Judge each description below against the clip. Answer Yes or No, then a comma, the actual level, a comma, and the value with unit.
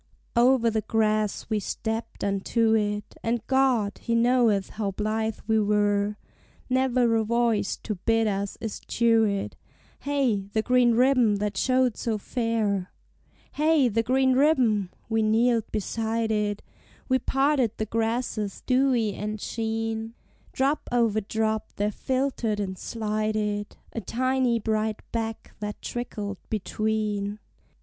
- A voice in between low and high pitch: No, high, 225 Hz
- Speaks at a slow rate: Yes, slow, 130 wpm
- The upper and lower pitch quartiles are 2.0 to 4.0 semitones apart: Yes, narrow, 2.4 semitones